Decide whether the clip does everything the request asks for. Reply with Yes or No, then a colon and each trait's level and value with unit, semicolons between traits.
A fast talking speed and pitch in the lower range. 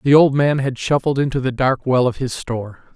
Yes: fast, 245 wpm; low, 130 Hz